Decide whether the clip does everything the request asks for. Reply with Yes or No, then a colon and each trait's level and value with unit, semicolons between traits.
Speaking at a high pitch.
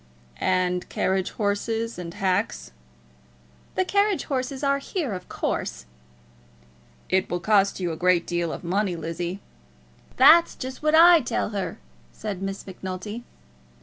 Yes: high, 195 Hz